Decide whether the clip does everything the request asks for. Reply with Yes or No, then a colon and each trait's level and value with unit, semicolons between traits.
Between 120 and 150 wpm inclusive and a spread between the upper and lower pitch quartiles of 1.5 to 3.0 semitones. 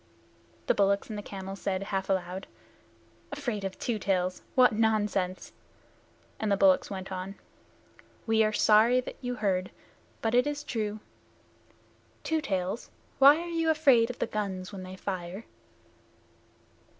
No: average, 145 wpm; average, 4.0 semitones